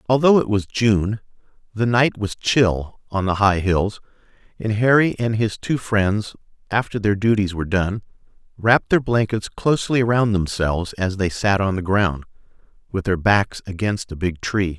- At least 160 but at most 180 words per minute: Yes, average, 170 wpm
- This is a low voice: Yes, low, 105 Hz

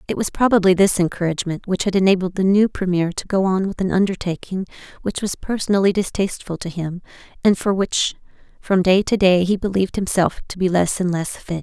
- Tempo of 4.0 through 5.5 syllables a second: No, 5.9 syllables/s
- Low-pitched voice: No, medium, 185 Hz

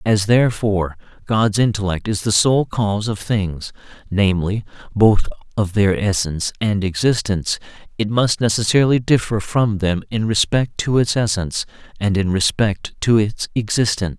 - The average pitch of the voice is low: Yes, low, 105 Hz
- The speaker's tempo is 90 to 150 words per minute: Yes, average, 145 wpm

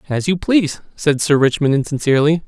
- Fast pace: No, average, 170 wpm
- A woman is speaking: No, male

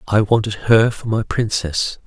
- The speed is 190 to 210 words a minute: No, average, 175 wpm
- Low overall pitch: Yes, low, 105 Hz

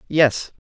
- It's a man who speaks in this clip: Yes, male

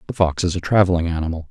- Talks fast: Yes, fast, 240 wpm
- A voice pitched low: Yes, very low, 90 Hz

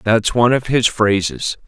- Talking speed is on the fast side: No, average, 180 wpm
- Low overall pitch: Yes, low, 110 Hz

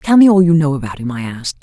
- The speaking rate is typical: No, fast, 335 wpm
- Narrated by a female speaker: Yes, female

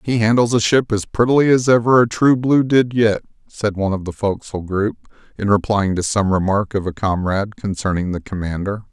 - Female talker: No, male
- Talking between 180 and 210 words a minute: Yes, average, 200 wpm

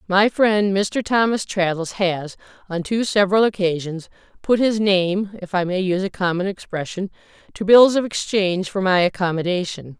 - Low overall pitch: No, high, 190 Hz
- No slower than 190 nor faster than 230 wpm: No, average, 160 wpm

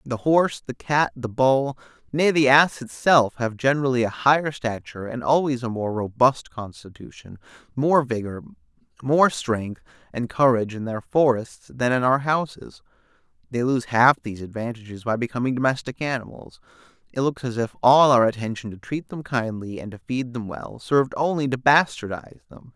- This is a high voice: No, low, 125 Hz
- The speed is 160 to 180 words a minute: Yes, average, 170 wpm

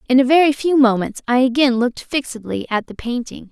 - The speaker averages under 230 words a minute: Yes, fast, 205 wpm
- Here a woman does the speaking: Yes, female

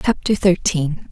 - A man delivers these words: No, female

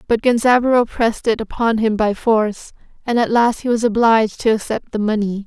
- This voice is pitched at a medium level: No, high, 225 Hz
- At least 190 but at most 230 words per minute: Yes, average, 200 wpm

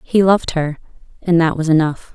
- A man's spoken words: No, female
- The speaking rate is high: No, average, 195 wpm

